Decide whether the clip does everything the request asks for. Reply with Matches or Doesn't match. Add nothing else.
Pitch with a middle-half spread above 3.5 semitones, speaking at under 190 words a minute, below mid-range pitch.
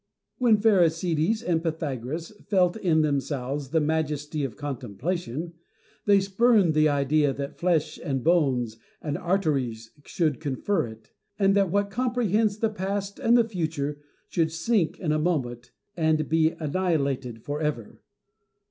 Doesn't match